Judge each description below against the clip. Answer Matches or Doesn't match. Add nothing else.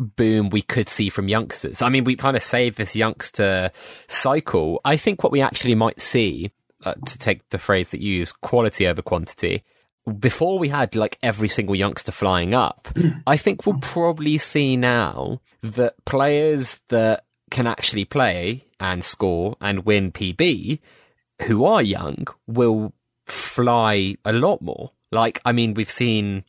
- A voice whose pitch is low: Matches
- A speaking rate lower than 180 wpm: Matches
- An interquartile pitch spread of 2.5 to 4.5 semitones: Matches